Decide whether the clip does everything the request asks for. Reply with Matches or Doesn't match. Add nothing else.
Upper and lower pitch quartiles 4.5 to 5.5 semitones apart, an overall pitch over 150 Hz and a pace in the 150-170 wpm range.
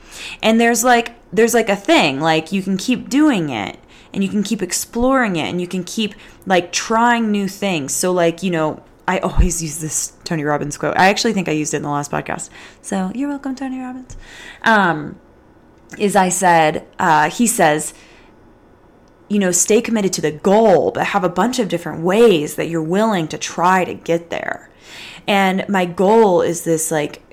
Doesn't match